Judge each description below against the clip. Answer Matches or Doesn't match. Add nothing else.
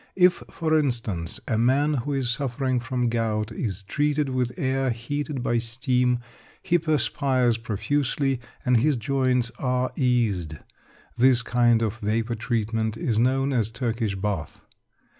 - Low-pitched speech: Matches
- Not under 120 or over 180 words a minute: Matches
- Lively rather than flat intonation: Doesn't match